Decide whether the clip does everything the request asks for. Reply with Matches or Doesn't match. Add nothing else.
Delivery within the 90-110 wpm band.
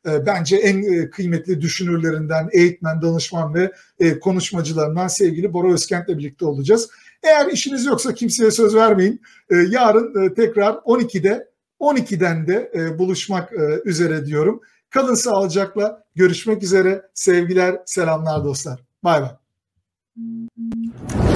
Matches